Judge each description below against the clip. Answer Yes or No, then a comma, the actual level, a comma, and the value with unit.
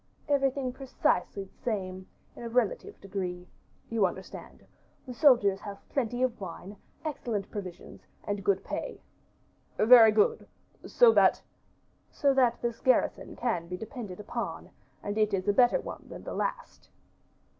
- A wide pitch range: No, average, 4.5 semitones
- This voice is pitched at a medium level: No, high, 220 Hz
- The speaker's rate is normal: Yes, average, 145 wpm